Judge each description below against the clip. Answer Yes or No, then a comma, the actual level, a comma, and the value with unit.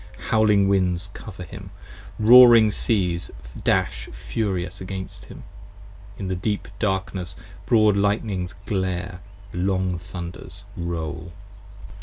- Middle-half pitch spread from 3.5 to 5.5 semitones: No, narrow, 2.6 semitones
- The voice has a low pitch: Yes, very low, 95 Hz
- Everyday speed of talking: No, slow, 100 wpm